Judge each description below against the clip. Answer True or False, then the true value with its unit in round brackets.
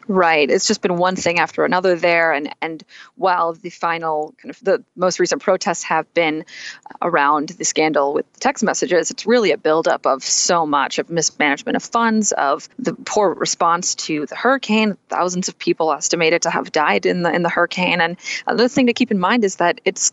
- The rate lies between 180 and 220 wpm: True (205 wpm)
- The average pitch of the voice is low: False (175 Hz)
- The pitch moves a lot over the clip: False (3.5 semitones)